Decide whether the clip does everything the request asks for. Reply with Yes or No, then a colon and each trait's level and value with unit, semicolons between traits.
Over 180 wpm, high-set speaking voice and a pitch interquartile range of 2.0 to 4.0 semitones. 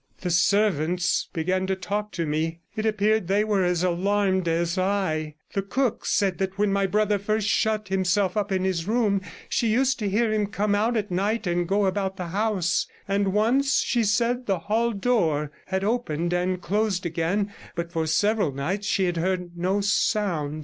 Yes: average, 190 wpm; high, 195 Hz; average, 3.0 semitones